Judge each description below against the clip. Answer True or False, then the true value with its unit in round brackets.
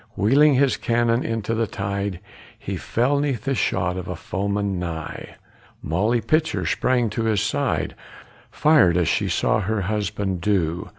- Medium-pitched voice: False (105 Hz)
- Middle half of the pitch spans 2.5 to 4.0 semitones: False (4.4 semitones)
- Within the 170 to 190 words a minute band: False (155 wpm)